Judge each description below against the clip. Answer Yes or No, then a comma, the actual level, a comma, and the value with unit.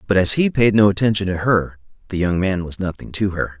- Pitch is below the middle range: Yes, very low, 95 Hz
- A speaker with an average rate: No, fast, 250 wpm